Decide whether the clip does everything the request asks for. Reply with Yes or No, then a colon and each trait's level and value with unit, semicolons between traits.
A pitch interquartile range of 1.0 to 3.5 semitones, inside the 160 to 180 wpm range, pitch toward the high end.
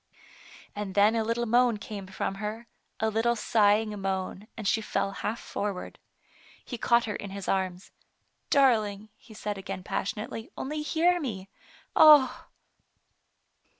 No: average, 3.2 semitones; average, 150 wpm; high, 215 Hz